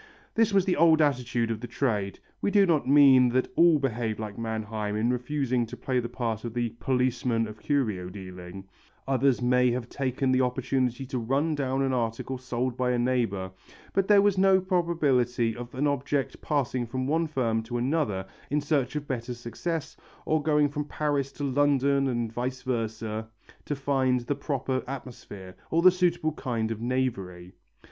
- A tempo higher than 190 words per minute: No, average, 175 wpm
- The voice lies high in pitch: No, low, 130 Hz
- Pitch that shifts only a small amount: No, average, 3.6 semitones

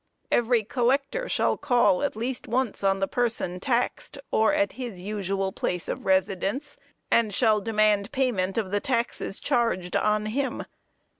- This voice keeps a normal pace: Yes, average, 150 wpm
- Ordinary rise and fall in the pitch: Yes, average, 4.1 semitones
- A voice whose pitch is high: Yes, high, 220 Hz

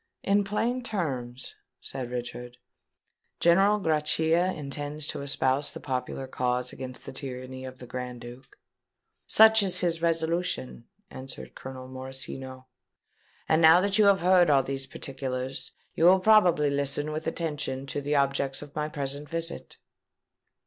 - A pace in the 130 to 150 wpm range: Yes, average, 140 wpm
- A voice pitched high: No, medium, 140 Hz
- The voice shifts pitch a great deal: No, average, 4.3 semitones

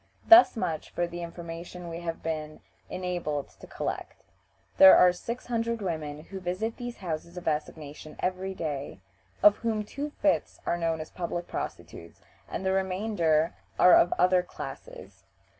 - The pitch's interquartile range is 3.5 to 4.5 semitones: No, average, 3.0 semitones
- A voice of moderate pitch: Yes, medium, 175 Hz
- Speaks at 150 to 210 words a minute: Yes, average, 155 wpm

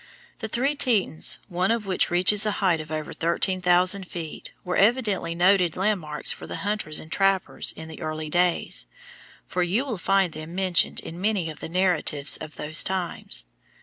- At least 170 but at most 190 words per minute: Yes, average, 180 wpm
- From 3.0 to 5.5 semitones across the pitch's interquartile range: Yes, average, 3.5 semitones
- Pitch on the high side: No, medium, 180 Hz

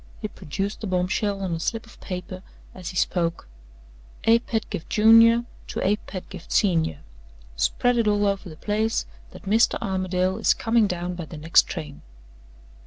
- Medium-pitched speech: No, high, 195 Hz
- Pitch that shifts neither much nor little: Yes, average, 3.7 semitones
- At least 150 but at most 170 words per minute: Yes, average, 165 wpm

